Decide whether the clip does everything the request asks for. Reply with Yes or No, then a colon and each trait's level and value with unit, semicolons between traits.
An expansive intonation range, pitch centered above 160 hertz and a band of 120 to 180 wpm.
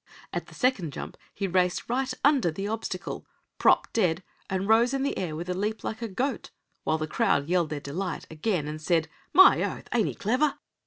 No: wide, 6.0 semitones; high, 190 Hz; fast, 205 wpm